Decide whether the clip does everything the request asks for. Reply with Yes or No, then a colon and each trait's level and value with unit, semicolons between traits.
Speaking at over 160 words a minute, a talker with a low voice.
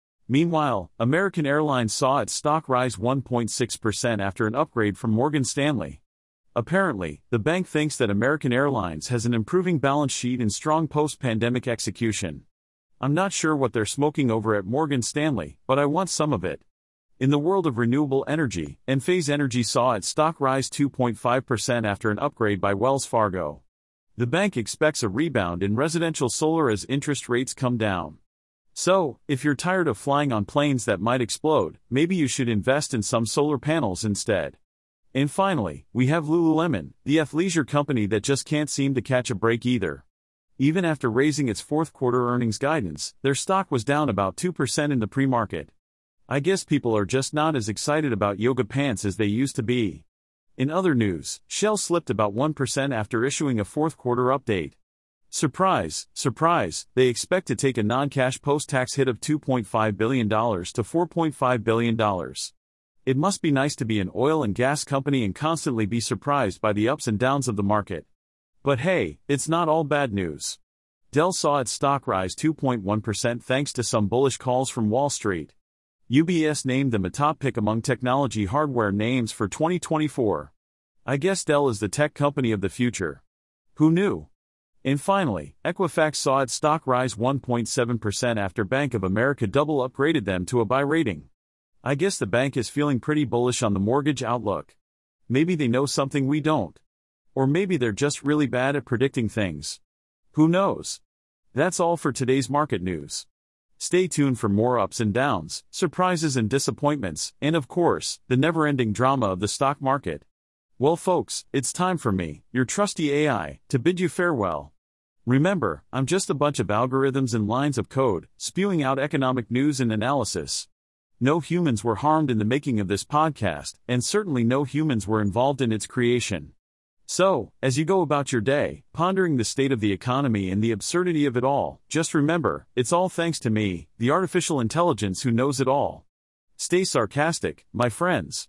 Yes: average, 180 wpm; low, 130 Hz